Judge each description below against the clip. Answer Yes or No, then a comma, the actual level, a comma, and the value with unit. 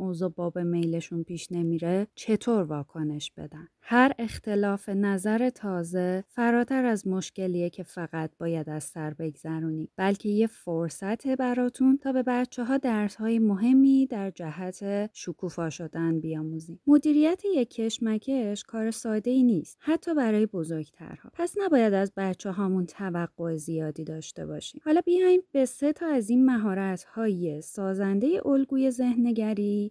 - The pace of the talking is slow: No, average, 135 wpm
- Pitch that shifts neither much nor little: No, wide, 6.5 semitones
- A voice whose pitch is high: Yes, high, 200 Hz